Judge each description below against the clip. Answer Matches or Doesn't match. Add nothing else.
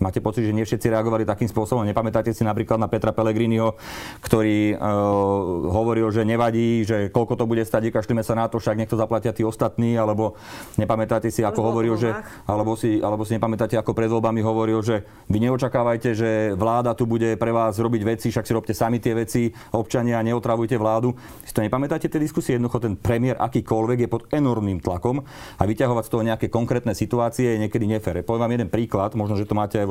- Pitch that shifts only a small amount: Matches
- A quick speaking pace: Matches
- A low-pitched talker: Matches